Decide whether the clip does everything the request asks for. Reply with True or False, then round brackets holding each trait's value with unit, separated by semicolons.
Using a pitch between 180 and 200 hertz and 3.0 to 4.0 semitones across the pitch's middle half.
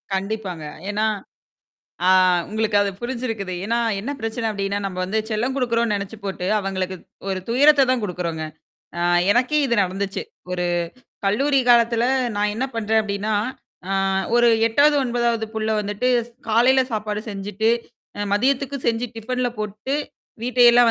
False (220 Hz; 3.3 semitones)